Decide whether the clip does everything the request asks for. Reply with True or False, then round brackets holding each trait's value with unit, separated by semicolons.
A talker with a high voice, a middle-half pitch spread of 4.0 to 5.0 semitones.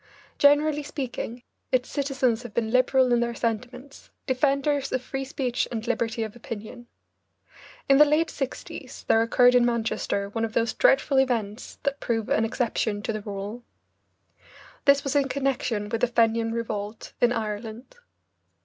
False (240 Hz; 3.2 semitones)